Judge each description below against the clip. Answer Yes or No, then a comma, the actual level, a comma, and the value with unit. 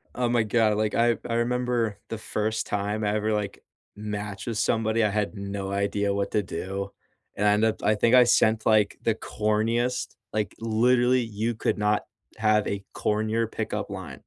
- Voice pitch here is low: Yes, low, 110 Hz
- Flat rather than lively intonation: Yes, narrow, 1.8 semitones